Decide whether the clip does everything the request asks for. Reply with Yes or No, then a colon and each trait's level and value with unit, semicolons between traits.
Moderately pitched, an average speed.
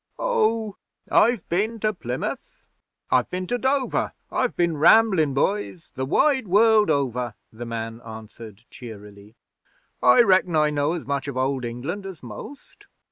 Yes: medium, 155 Hz; average, 145 wpm